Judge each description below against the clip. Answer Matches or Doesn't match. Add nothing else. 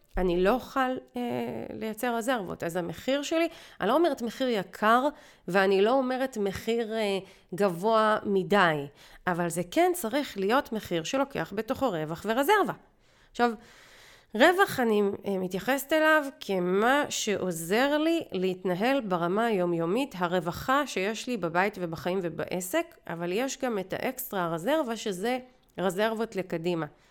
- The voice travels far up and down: Matches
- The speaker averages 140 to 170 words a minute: Doesn't match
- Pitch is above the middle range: Matches